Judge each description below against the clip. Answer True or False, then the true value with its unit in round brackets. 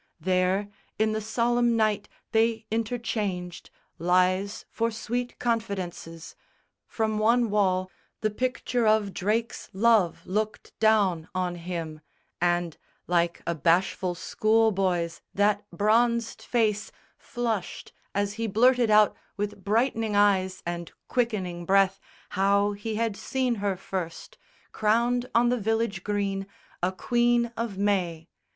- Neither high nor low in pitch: False (205 Hz)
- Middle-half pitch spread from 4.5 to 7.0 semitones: False (3.5 semitones)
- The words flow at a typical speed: False (120 wpm)